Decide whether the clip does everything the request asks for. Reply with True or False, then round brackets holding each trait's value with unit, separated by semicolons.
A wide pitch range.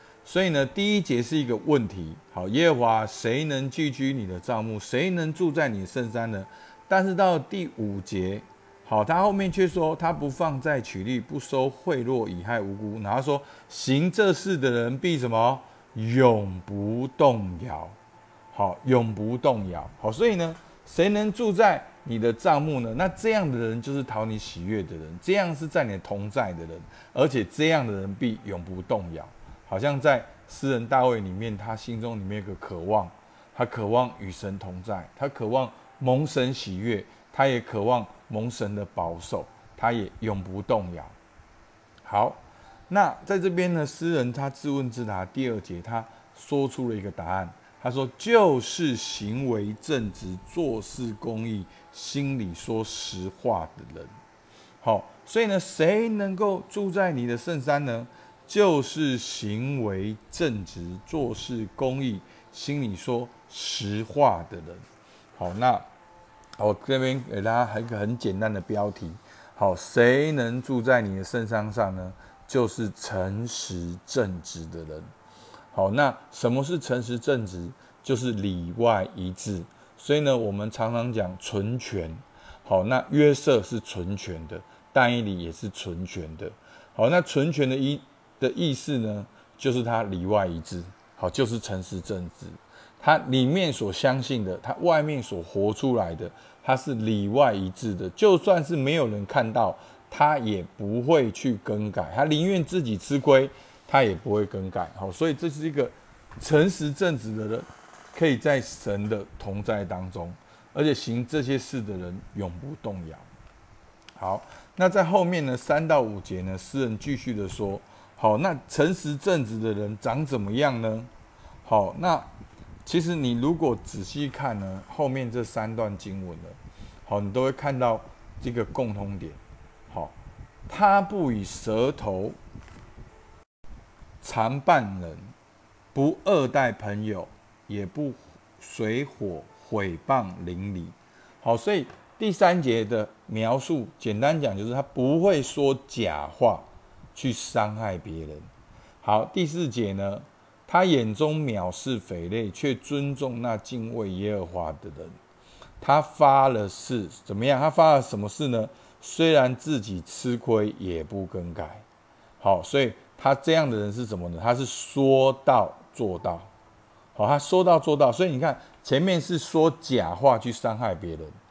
True (5.7 semitones)